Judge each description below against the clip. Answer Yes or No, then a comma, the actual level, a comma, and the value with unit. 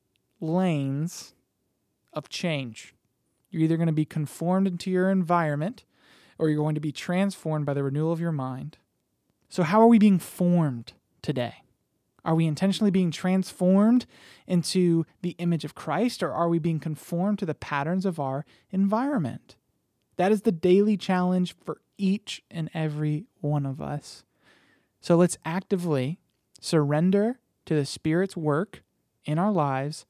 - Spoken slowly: No, average, 150 wpm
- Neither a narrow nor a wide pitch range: Yes, average, 3.8 semitones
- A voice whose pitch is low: No, medium, 170 Hz